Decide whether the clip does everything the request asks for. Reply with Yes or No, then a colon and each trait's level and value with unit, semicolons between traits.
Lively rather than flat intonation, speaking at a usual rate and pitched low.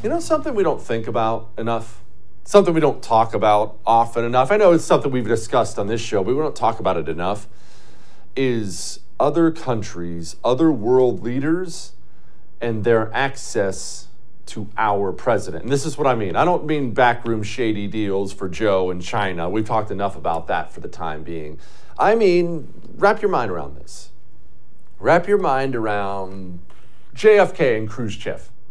Yes: wide, 6.3 semitones; average, 170 wpm; low, 115 Hz